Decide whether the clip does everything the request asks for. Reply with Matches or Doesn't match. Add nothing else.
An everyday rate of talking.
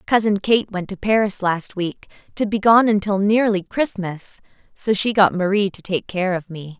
Matches